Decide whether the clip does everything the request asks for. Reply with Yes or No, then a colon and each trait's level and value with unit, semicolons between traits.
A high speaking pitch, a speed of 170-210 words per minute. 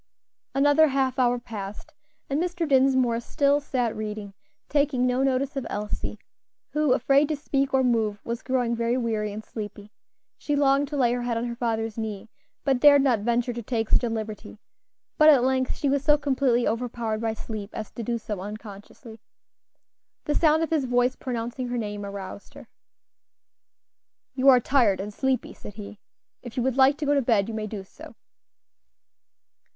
Yes: high, 245 Hz; average, 180 wpm